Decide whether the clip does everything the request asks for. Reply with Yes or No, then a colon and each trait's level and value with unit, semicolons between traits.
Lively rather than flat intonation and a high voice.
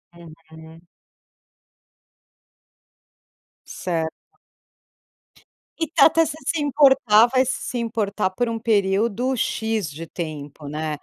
Yes: wide, 7.6 semitones; high, 210 Hz